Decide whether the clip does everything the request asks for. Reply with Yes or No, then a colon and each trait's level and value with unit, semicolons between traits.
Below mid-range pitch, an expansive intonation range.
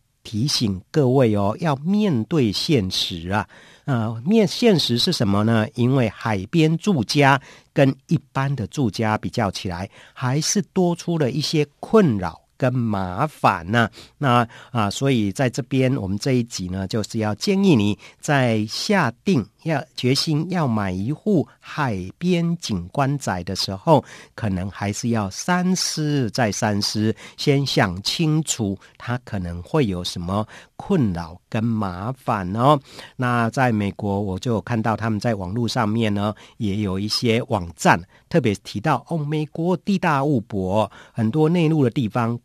Yes: low, 120 Hz; wide, 6.2 semitones